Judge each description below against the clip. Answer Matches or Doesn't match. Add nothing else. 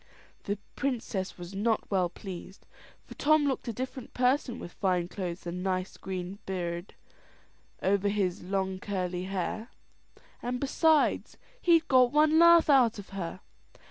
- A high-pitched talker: Matches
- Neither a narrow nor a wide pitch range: Doesn't match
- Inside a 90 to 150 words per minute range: Matches